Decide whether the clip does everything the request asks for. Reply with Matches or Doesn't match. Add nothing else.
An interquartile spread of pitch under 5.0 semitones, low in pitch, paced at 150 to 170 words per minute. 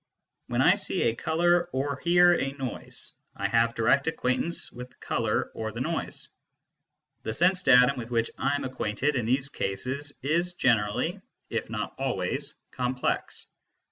Doesn't match